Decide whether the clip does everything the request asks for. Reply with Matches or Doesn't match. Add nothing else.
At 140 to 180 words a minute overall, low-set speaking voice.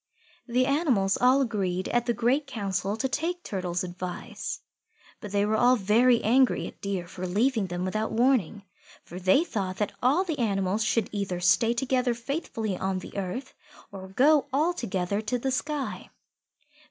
Doesn't match